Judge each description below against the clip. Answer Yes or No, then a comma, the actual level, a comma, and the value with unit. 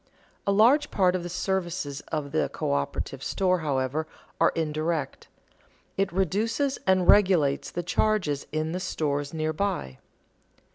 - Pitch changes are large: No, average, 4.2 semitones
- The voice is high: No, medium, 170 Hz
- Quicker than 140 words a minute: No, slow, 135 wpm